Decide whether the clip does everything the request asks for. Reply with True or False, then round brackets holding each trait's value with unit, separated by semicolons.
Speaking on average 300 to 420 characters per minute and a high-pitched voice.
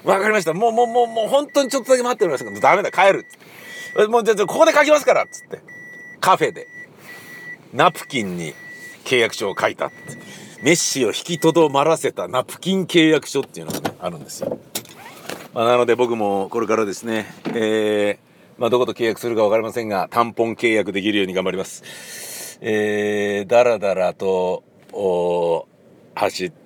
False (355 characters per minute; 120 Hz)